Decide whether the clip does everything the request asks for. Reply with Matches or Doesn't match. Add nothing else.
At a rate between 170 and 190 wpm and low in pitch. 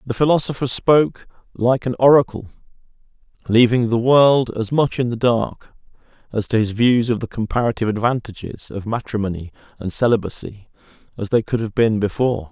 Doesn't match